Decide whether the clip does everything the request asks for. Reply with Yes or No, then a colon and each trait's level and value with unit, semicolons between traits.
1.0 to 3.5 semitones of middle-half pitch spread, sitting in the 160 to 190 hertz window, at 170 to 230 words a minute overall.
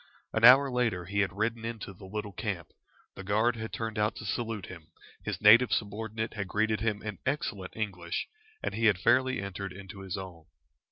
No: average, 2.7 semitones; low, 105 Hz; average, 190 wpm